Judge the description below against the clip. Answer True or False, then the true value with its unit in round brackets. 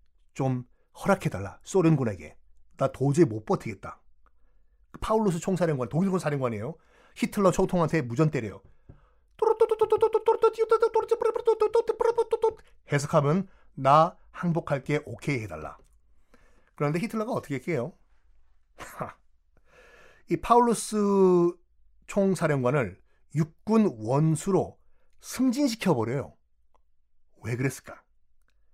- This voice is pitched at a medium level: True (160 Hz)